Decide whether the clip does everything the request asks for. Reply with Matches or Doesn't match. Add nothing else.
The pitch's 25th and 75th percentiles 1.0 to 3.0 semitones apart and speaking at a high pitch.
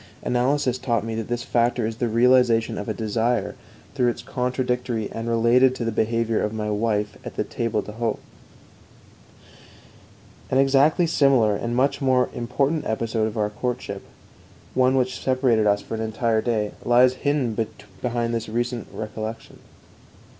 Doesn't match